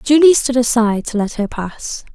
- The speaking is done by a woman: Yes, female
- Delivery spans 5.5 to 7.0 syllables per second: No, 5.0 syllables/s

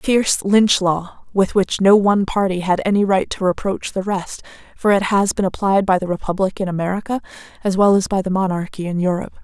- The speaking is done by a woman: Yes, female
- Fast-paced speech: Yes, fast, 210 wpm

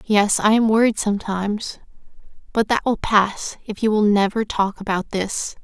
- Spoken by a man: No, female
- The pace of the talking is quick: No, average, 170 wpm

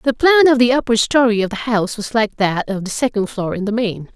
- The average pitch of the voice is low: No, high, 225 Hz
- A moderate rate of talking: No, fast, 275 wpm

